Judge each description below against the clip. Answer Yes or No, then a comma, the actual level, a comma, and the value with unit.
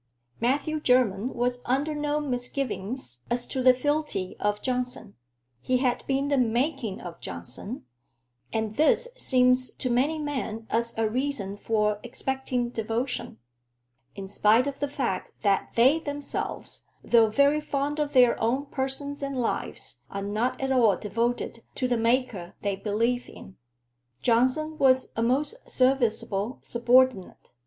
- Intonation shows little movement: No, average, 3.6 semitones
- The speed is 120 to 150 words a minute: Yes, average, 140 wpm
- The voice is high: Yes, very high, 250 Hz